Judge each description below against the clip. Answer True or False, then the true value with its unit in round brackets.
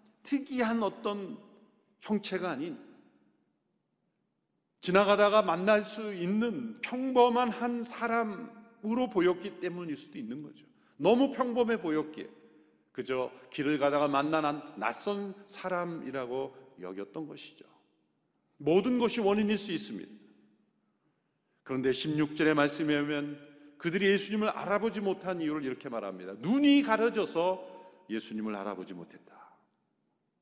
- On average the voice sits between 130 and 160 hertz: False (190 Hz)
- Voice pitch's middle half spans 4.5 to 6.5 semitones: False (7.5 semitones)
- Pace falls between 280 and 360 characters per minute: False (260 characters per minute)